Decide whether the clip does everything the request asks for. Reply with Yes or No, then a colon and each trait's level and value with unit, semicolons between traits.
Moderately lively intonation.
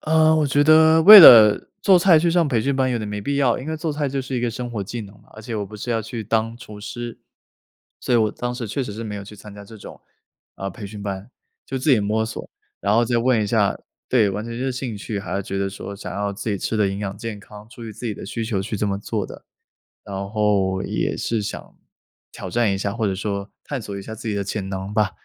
Yes: average, 3.5 semitones